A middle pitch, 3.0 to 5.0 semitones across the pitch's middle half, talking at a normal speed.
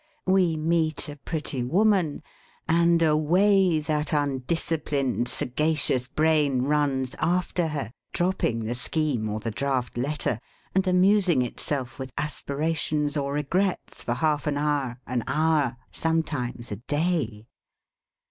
No: medium, 150 Hz; average, 3.8 semitones; slow, 120 wpm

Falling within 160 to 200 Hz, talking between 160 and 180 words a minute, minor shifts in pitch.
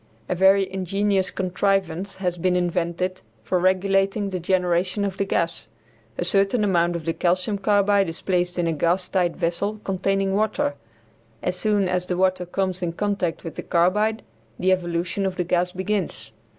Yes: medium, 185 Hz; average, 170 wpm; narrow, 1.9 semitones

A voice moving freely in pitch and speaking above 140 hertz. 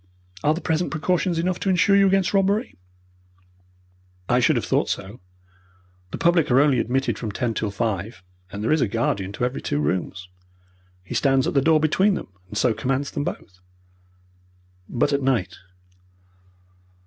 No: wide, 7.6 semitones; low, 135 Hz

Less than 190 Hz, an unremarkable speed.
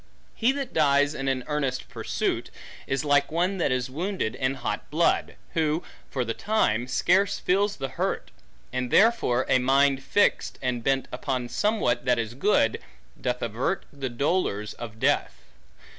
Yes: low, 135 Hz; average, 160 wpm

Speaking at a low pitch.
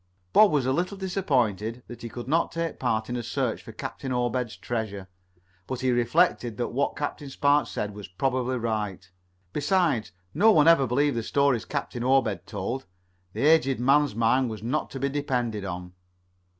Yes: low, 125 Hz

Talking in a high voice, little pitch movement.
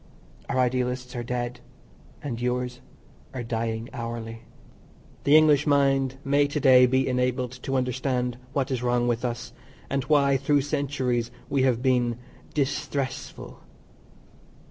No: low, 125 Hz; narrow, 2.1 semitones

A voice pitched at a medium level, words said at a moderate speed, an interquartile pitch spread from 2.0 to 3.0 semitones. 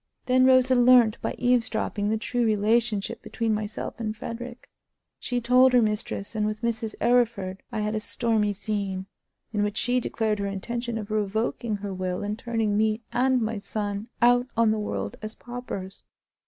No: high, 220 Hz; average, 170 wpm; narrow, 2.5 semitones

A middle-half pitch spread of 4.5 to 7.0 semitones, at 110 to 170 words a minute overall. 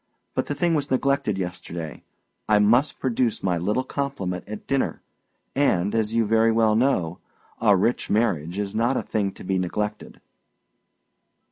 Yes: average, 5.1 semitones; average, 155 wpm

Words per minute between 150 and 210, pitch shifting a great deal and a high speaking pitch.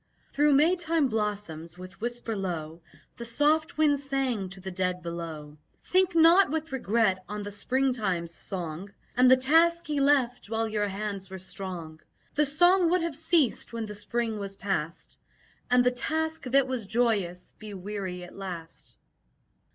Yes: average, 160 wpm; wide, 7.1 semitones; high, 220 Hz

